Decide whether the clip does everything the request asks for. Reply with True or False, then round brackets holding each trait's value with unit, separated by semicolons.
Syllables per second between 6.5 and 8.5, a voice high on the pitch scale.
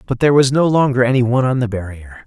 False (7.3 syllables/s; 125 Hz)